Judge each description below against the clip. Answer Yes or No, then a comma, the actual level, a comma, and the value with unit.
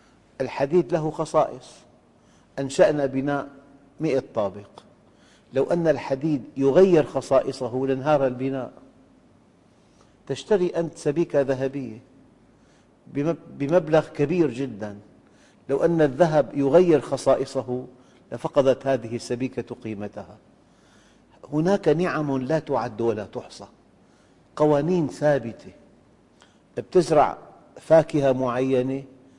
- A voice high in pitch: No, low, 135 Hz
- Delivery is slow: Yes, slow, 85 wpm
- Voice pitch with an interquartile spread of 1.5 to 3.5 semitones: Yes, average, 3.0 semitones